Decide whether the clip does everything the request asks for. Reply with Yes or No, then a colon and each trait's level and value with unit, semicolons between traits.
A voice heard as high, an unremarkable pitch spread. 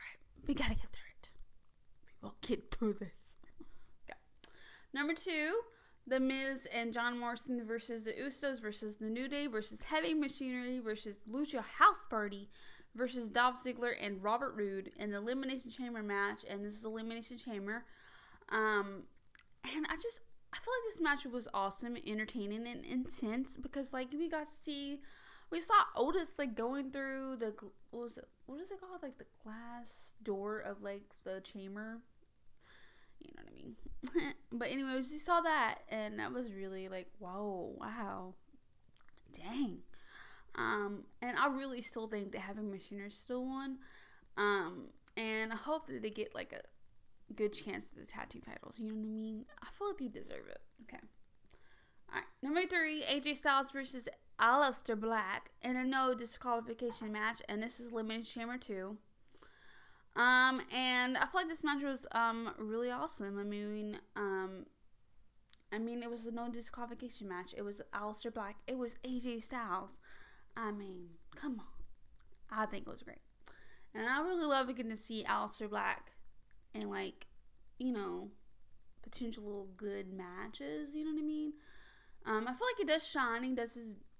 Yes: high, 240 Hz; average, 4.2 semitones